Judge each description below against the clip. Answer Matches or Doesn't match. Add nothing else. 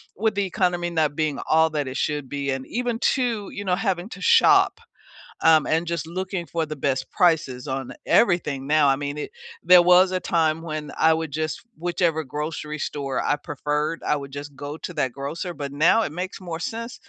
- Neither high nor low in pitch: Matches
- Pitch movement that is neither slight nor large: Matches